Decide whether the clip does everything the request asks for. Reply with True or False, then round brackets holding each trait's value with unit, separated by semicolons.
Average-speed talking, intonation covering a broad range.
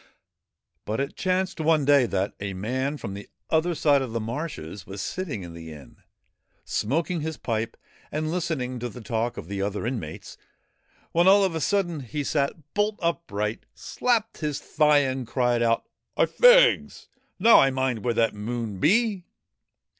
True (175 wpm; 7.0 semitones)